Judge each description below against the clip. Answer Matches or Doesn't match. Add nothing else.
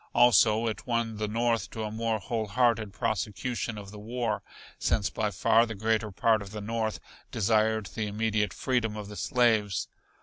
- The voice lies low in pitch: Matches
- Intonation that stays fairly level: Matches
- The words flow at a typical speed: Matches